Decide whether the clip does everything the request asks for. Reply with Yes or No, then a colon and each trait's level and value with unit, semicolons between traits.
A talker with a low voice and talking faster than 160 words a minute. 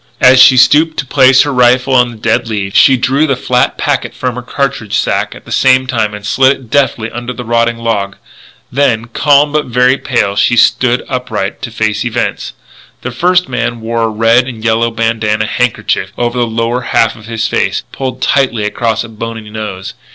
Yes: low, 120 Hz; average, 195 wpm